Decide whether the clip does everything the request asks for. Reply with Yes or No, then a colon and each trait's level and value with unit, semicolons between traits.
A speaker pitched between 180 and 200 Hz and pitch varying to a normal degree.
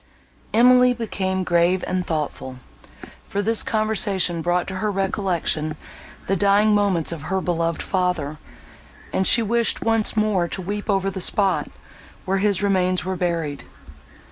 Yes: high, 190 Hz; average, 3.0 semitones